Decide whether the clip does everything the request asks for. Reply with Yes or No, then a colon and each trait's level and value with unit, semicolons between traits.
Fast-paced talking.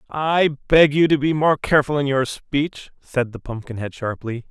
No: average, 185 wpm